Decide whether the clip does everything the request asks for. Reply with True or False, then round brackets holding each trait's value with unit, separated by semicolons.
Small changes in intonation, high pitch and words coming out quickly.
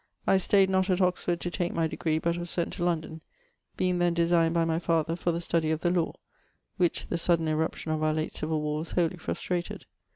False (1.6 semitones; 170 Hz; 220 wpm)